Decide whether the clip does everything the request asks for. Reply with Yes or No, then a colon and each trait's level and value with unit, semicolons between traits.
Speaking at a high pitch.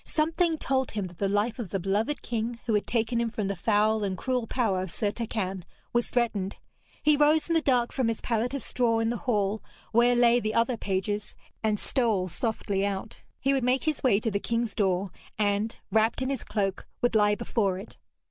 Yes: high, 225 Hz